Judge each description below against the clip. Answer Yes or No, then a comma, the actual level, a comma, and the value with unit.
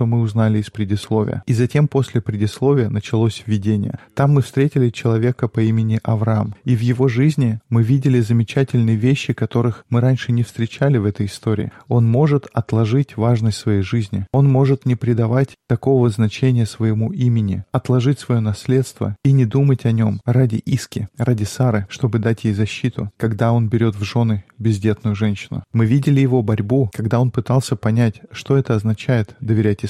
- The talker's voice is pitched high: No, low, 115 Hz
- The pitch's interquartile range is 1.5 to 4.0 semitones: Yes, average, 2.8 semitones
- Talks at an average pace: No, fast, 165 wpm